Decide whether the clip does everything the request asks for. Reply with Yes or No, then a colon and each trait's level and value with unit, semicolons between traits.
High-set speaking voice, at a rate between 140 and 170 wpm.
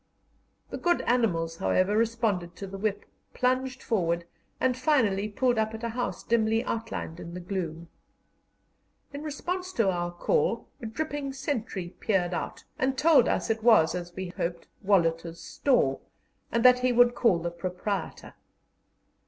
Yes: high, 220 Hz; average, 155 wpm